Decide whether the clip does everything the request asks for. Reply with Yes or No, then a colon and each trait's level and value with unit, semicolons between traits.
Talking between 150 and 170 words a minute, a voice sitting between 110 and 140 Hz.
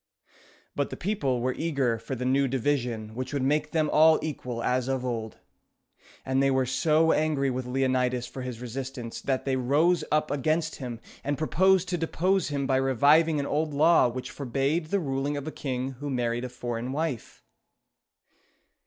No: average, 180 wpm; low, 135 Hz